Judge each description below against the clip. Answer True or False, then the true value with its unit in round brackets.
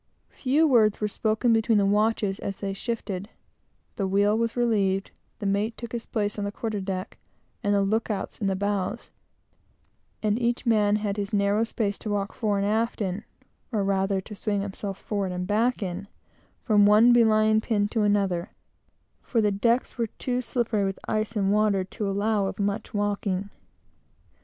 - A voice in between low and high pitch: False (205 Hz)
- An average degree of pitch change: False (2.0 semitones)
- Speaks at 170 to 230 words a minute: True (175 wpm)